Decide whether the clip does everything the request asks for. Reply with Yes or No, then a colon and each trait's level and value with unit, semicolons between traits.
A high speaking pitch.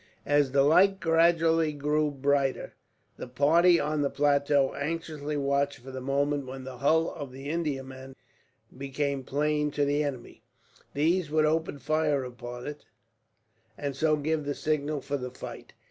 No: medium, 145 Hz